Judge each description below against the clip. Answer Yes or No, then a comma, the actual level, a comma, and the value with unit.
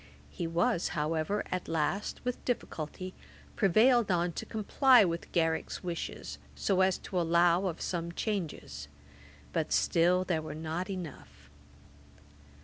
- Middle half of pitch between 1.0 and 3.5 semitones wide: Yes, average, 2.8 semitones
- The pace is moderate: No, slow, 130 wpm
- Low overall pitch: No, medium, 175 Hz